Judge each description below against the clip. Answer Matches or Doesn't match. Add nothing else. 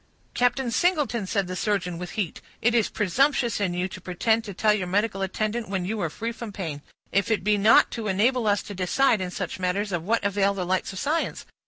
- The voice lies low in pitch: Doesn't match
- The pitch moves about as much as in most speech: Matches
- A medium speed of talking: Doesn't match